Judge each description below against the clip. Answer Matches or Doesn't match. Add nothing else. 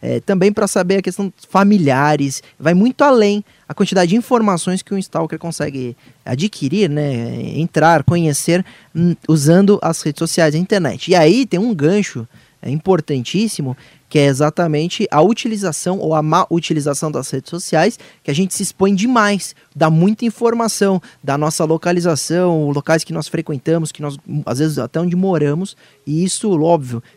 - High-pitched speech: Doesn't match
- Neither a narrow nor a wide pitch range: Matches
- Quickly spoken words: Doesn't match